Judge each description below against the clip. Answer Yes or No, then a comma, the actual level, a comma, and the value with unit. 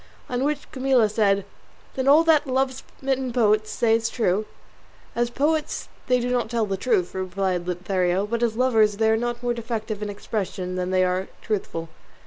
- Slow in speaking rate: No, average, 180 wpm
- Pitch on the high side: Yes, high, 225 Hz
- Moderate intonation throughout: Yes, average, 4.3 semitones